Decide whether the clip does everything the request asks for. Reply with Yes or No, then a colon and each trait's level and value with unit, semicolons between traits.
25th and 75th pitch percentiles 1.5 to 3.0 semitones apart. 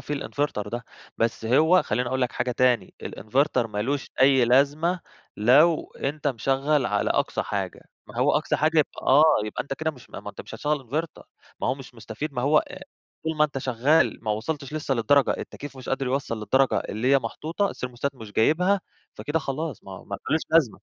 No: average, 3.8 semitones